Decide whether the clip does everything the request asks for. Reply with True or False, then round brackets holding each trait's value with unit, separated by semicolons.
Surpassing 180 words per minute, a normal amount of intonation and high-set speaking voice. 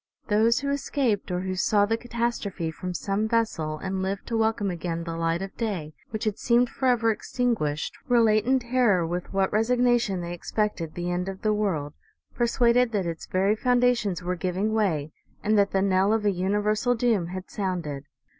True (190 wpm; 4.2 semitones; 205 Hz)